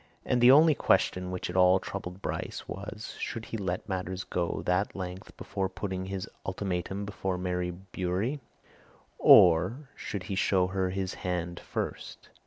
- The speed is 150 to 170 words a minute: Yes, average, 160 wpm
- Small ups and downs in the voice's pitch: Yes, narrow, 1.6 semitones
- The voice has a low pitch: Yes, very low, 95 Hz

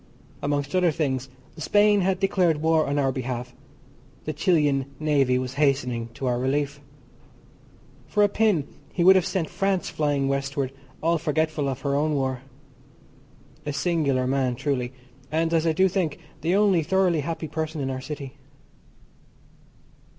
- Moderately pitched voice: Yes, medium, 150 Hz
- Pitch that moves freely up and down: No, average, 3.7 semitones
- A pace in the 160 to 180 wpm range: No, average, 150 wpm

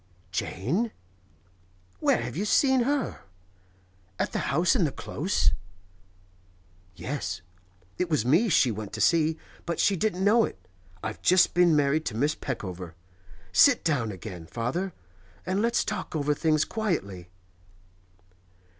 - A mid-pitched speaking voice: Yes, medium, 155 Hz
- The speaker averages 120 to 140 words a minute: Yes, slow, 135 wpm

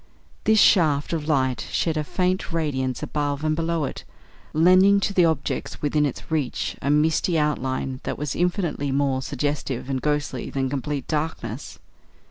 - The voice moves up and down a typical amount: Yes, average, 3.2 semitones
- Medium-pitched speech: Yes, medium, 150 Hz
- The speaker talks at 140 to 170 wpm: Yes, average, 155 wpm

